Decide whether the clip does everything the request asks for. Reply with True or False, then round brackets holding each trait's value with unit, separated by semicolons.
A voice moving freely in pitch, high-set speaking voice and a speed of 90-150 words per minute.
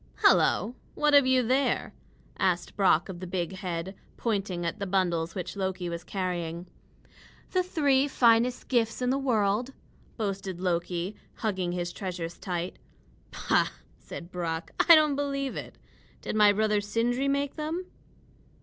True (6.1 semitones; 200 Hz; 145 wpm)